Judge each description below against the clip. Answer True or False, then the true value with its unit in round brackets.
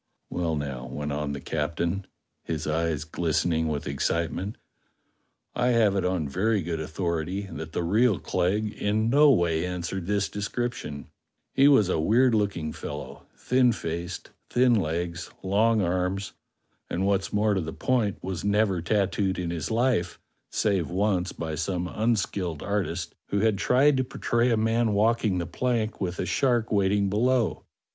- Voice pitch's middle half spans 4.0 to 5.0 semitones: True (4.6 semitones)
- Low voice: True (95 Hz)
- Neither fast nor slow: True (155 wpm)